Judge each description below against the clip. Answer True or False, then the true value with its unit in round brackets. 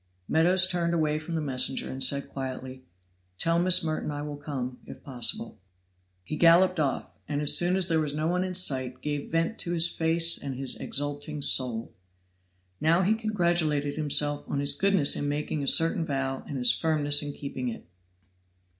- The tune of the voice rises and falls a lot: False (3.3 semitones)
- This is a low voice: False (150 Hz)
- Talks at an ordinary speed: True (185 wpm)